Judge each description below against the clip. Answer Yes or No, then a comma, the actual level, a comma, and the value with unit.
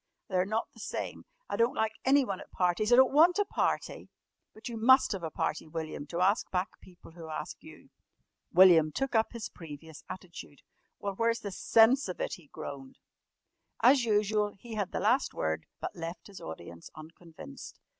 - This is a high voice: Yes, high, 195 Hz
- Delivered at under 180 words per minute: No, average, 185 wpm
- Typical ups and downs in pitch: No, wide, 5.8 semitones